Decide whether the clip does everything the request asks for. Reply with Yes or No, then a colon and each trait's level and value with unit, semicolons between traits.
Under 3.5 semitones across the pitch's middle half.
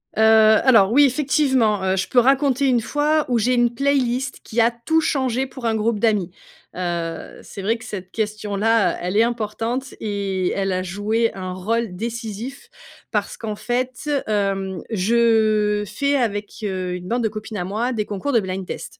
No: average, 3.8 semitones